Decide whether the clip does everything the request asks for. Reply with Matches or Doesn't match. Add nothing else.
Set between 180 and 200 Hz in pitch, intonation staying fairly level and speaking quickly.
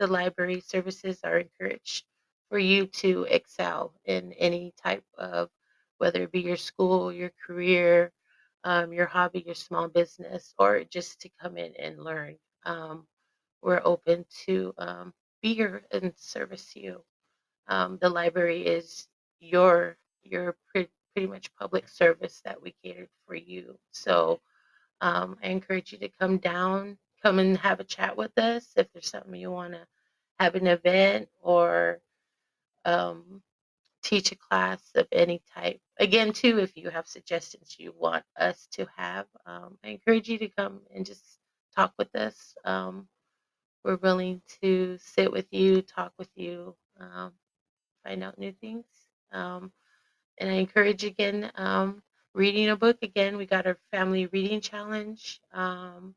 Doesn't match